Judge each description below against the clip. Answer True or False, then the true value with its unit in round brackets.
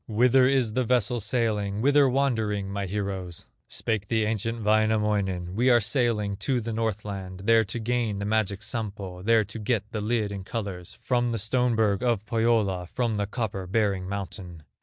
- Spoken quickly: False (175 wpm)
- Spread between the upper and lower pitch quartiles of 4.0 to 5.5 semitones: False (2.8 semitones)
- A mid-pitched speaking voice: False (110 Hz)